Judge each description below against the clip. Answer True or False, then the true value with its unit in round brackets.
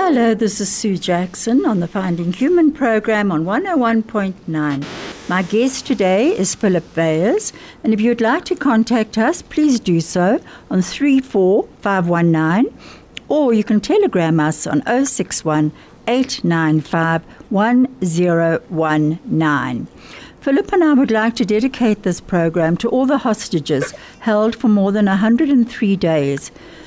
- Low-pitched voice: False (210 Hz)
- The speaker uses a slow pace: True (130 wpm)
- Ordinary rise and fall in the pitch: False (6.2 semitones)